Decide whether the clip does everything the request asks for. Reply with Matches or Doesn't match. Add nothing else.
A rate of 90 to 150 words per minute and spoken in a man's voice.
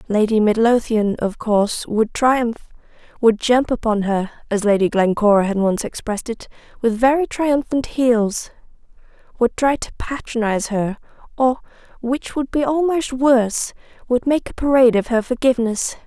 Doesn't match